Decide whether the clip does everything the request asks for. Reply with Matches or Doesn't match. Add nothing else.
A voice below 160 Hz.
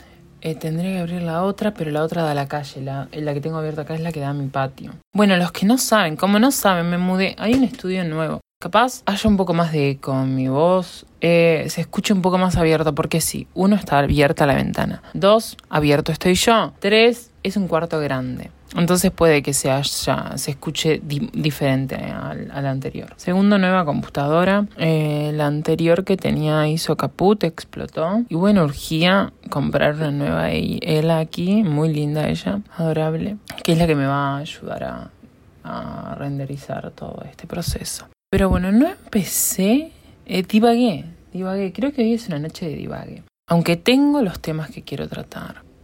Doesn't match